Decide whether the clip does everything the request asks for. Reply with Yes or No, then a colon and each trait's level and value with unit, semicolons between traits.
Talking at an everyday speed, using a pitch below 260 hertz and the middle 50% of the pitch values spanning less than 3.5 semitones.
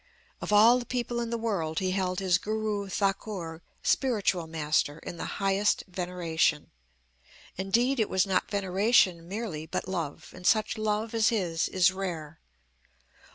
No: average, 150 wpm; high, 190 Hz; average, 4.1 semitones